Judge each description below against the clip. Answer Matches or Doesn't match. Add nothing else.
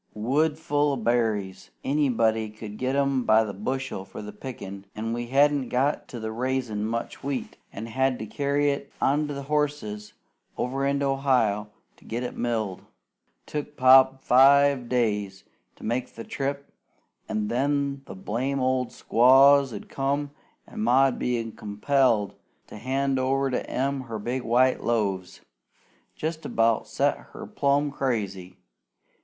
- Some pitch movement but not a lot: Matches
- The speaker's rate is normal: Matches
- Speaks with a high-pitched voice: Doesn't match